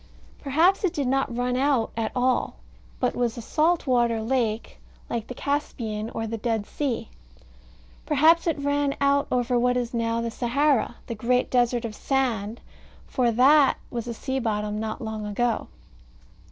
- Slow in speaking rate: No, average, 165 wpm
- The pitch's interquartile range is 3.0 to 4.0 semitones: Yes, average, 3.3 semitones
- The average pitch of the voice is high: Yes, high, 245 Hz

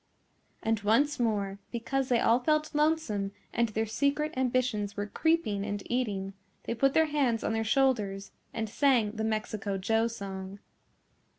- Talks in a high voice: Yes, high, 225 Hz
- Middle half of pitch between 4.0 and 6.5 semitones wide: Yes, average, 4.6 semitones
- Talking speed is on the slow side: No, average, 155 wpm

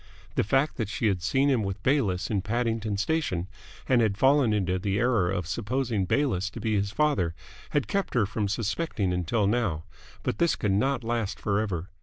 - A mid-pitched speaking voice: No, low, 105 Hz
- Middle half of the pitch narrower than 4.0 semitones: No, average, 4.4 semitones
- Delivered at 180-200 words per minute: Yes, average, 190 wpm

